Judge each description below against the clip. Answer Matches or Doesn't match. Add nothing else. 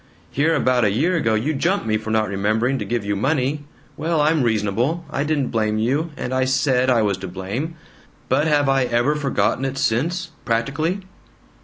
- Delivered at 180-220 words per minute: Matches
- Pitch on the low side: Matches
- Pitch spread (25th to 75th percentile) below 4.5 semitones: Doesn't match